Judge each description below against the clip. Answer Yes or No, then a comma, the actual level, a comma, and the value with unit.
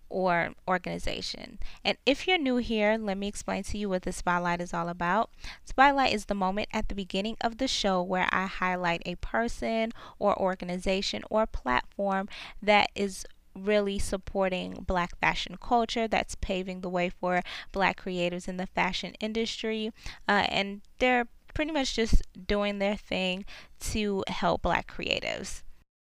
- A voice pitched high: Yes, high, 195 Hz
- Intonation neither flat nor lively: Yes, average, 3.2 semitones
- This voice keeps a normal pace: Yes, average, 155 wpm